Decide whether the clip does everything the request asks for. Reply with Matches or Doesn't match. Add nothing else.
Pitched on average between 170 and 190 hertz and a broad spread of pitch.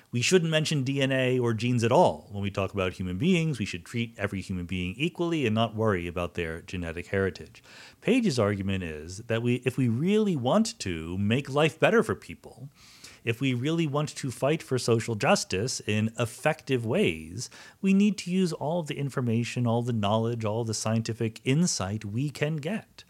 Doesn't match